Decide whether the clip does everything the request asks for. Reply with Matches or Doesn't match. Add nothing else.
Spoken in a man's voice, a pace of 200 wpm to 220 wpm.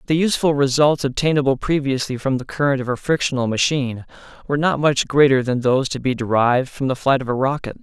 Matches